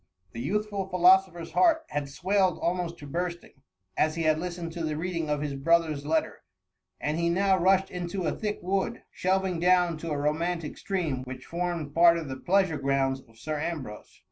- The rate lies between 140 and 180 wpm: No, average, 190 wpm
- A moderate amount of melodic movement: Yes, average, 3.4 semitones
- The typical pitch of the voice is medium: Yes, medium, 170 Hz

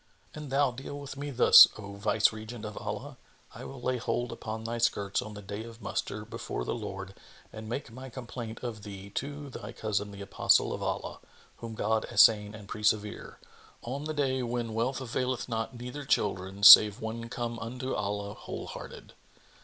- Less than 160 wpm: No, average, 175 wpm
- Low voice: Yes, low, 115 Hz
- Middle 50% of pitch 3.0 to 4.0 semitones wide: Yes, average, 3.4 semitones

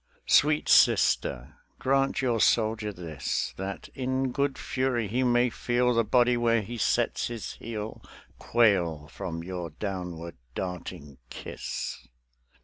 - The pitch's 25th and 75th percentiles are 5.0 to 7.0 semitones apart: Yes, wide, 5.4 semitones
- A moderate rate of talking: No, slow, 125 wpm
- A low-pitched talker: Yes, low, 110 Hz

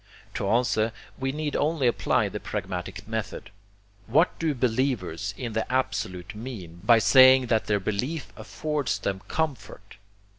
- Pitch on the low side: Yes, low, 115 Hz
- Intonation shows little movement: No, average, 4.8 semitones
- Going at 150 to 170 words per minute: No, average, 140 wpm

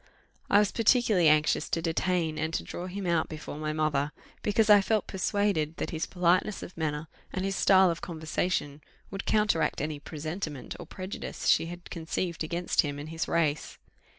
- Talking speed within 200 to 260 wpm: No, average, 180 wpm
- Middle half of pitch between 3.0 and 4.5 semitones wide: Yes, average, 3.6 semitones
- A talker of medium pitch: Yes, medium, 170 Hz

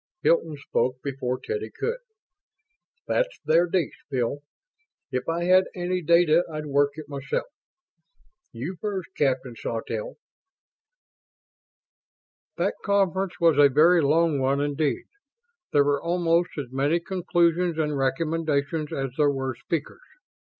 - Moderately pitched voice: Yes, medium, 155 Hz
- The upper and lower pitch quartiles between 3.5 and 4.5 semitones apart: Yes, average, 3.8 semitones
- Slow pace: Yes, slow, 120 wpm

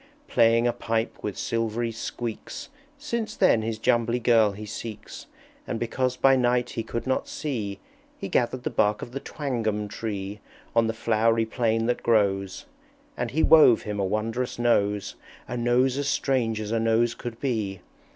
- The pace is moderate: Yes, average, 170 wpm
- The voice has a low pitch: Yes, low, 115 Hz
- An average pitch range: No, narrow, 2.2 semitones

